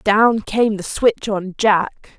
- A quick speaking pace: No, average, 165 wpm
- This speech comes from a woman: Yes, female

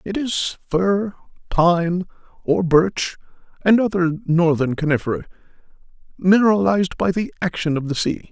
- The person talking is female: No, male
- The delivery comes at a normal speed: No, slow, 125 wpm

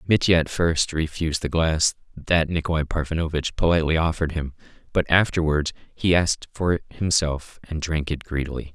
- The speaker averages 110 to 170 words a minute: Yes, average, 160 wpm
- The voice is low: Yes, very low, 80 Hz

